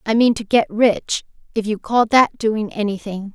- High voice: Yes, high, 220 Hz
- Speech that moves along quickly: No, average, 195 wpm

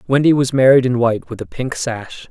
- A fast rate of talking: Yes, fast, 235 wpm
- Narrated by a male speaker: Yes, male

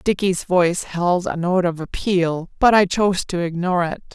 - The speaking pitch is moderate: Yes, medium, 180 Hz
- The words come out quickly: No, average, 190 wpm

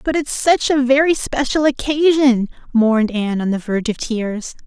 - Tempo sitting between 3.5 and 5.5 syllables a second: Yes, 5.0 syllables/s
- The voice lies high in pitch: Yes, very high, 255 Hz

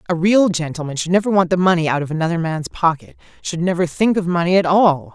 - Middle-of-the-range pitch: Yes, medium, 175 Hz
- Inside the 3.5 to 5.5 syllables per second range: No, 6.2 syllables/s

